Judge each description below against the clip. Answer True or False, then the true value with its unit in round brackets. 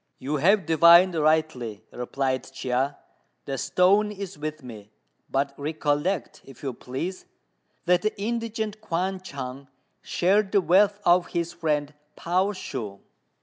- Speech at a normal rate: False (130 wpm)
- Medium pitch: True (160 Hz)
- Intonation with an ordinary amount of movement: False (5.7 semitones)